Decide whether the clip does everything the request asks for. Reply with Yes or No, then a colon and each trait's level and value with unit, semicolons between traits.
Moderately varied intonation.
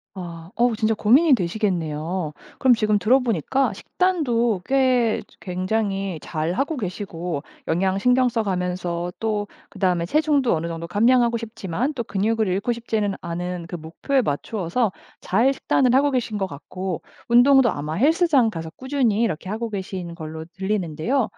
No: wide, 5.7 semitones